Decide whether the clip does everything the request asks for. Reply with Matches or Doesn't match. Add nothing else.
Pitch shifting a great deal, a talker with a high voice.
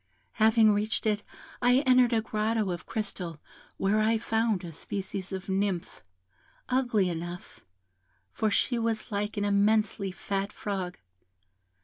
Doesn't match